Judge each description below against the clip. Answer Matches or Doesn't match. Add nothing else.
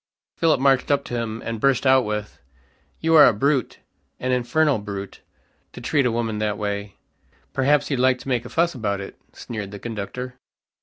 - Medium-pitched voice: Doesn't match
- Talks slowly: Doesn't match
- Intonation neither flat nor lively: Matches